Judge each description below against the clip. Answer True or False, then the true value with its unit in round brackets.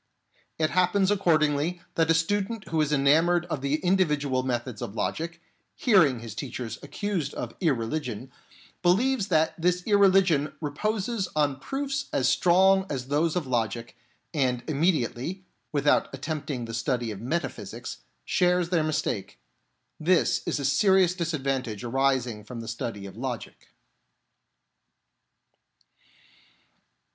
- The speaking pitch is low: False (155 Hz)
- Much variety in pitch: True (5.8 semitones)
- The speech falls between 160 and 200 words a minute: False (135 wpm)